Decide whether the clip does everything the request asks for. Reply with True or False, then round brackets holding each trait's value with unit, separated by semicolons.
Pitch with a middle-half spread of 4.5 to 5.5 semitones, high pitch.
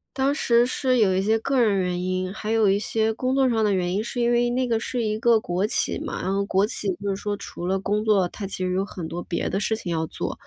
False (3.8 semitones; 210 Hz)